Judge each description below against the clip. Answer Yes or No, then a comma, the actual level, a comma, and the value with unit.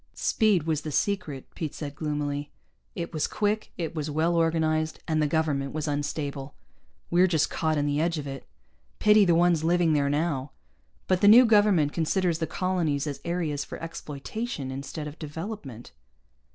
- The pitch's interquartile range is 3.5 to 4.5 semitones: No, average, 3.1 semitones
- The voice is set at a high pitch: No, medium, 155 Hz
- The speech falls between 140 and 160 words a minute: No, average, 170 wpm